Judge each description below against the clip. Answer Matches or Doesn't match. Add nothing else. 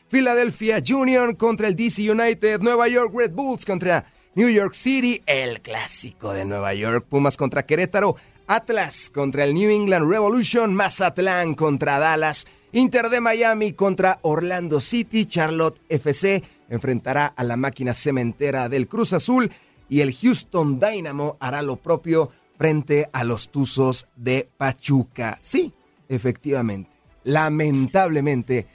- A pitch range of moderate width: Doesn't match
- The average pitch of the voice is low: Doesn't match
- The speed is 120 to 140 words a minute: Matches